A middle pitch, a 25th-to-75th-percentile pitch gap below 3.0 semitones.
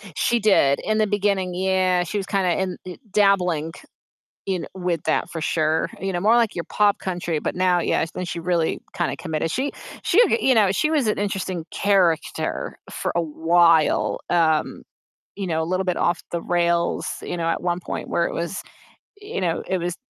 Yes: medium, 180 Hz; narrow, 2.6 semitones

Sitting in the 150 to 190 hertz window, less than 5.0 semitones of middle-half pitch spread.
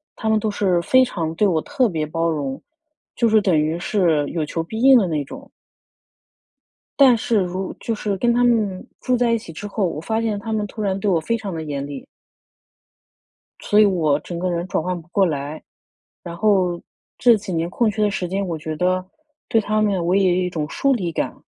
Yes: medium, 185 Hz; average, 4.6 semitones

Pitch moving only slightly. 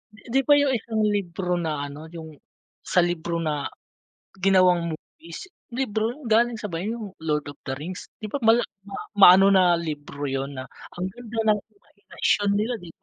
No: average, 5.1 semitones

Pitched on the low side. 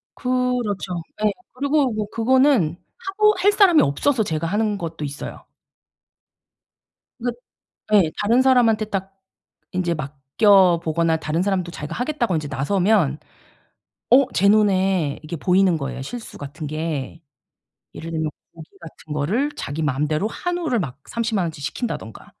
No: medium, 185 Hz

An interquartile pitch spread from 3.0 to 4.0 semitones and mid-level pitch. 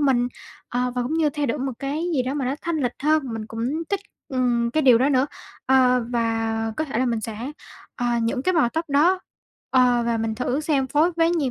No: average, 3.7 semitones; very high, 255 Hz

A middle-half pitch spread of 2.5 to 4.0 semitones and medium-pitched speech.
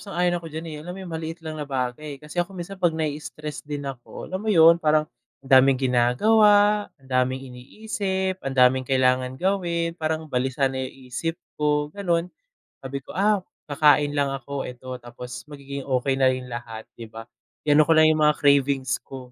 No: average, 4.4 semitones; medium, 145 Hz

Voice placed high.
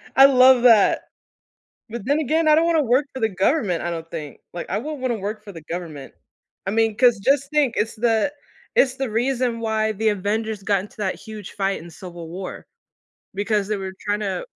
Yes: high, 220 Hz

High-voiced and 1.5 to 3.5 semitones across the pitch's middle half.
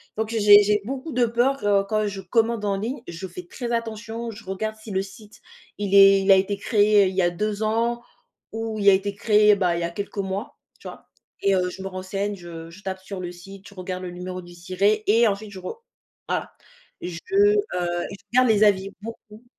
Yes: high, 200 Hz; narrow, 2.6 semitones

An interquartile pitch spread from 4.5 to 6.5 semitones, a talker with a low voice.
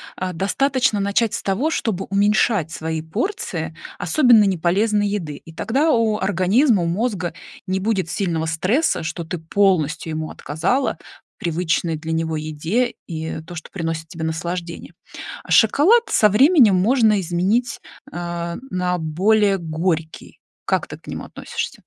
No: average, 5.0 semitones; medium, 185 Hz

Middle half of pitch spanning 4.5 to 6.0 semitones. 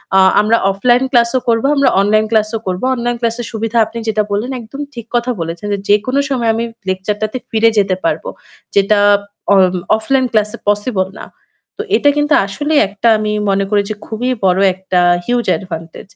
No: average, 3.1 semitones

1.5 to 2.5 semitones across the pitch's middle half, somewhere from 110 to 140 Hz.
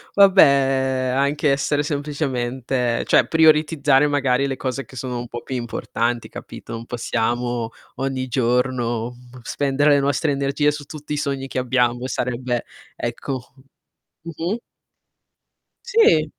No: average, 2.9 semitones; low, 135 Hz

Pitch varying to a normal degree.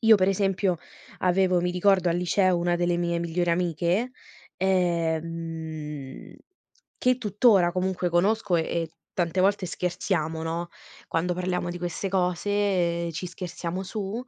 No: narrow, 2.0 semitones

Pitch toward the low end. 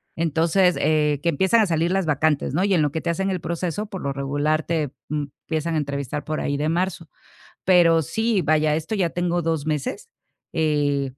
No: medium, 160 Hz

